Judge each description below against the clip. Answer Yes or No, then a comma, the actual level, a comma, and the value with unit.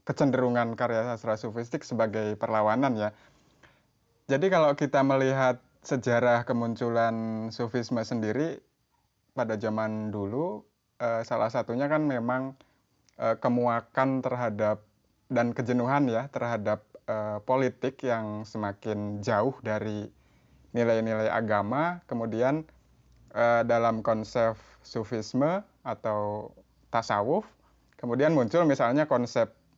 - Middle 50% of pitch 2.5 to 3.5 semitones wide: Yes, average, 2.8 semitones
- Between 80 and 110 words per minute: Yes, average, 90 wpm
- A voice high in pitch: No, low, 115 Hz